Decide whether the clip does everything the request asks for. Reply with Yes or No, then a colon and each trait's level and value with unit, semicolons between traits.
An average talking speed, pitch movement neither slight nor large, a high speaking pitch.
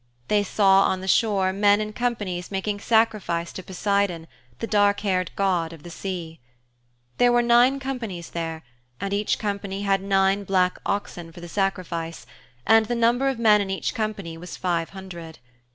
Yes: average, 170 wpm; average, 3.1 semitones; high, 195 Hz